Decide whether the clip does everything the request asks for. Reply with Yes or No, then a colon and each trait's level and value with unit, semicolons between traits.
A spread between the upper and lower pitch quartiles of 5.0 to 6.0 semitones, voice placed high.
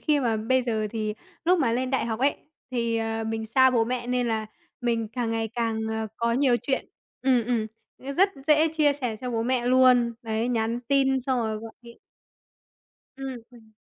No: narrow, 2.5 semitones; high, 240 Hz